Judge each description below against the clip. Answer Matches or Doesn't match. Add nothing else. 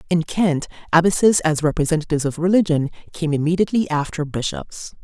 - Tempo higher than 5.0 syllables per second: Matches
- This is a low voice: Doesn't match